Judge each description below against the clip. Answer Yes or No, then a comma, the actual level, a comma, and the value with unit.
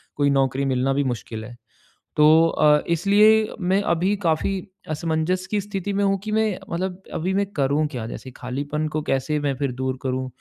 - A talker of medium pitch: Yes, medium, 155 Hz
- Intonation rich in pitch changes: Yes, wide, 6.1 semitones